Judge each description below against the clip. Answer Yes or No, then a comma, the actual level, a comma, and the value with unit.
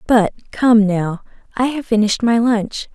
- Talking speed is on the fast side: No, average, 165 wpm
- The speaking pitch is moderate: No, high, 225 Hz